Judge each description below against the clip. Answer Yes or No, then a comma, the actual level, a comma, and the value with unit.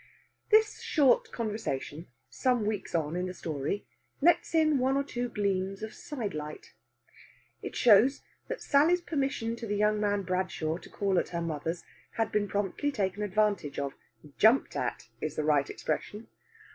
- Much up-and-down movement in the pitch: Yes, wide, 6.1 semitones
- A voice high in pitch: Yes, high, 205 Hz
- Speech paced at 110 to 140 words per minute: No, average, 160 wpm